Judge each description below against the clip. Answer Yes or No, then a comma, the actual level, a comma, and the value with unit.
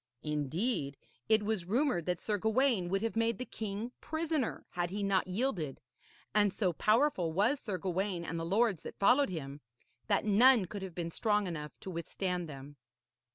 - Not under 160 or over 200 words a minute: Yes, average, 175 wpm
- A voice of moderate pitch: No, high, 195 Hz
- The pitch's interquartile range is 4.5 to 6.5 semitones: Yes, average, 4.8 semitones